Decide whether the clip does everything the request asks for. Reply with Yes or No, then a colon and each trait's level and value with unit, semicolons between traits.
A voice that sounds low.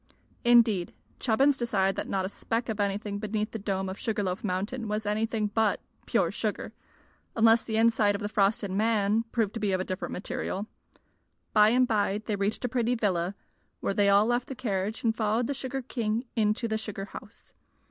No: high, 215 Hz